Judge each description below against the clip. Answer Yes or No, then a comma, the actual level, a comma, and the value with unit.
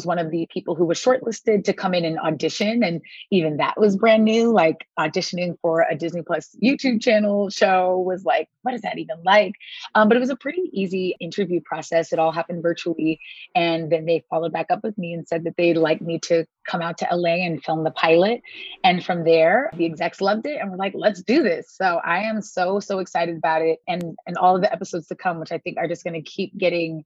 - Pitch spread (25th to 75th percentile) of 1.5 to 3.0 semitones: No, average, 3.9 semitones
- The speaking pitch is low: No, medium, 175 Hz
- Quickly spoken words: Yes, fast, 240 wpm